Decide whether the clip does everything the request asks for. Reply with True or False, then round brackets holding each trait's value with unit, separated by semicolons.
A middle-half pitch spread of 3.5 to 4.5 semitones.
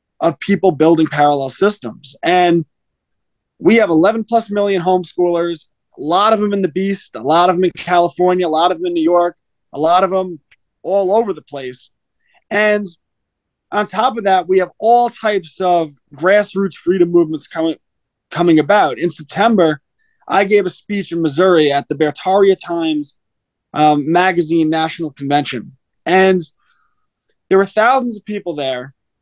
True (4.0 semitones)